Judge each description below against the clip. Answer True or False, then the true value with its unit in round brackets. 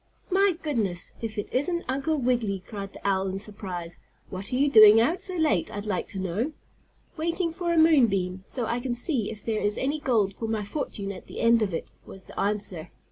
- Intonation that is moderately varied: False (6.2 semitones)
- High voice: True (220 Hz)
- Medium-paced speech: False (220 wpm)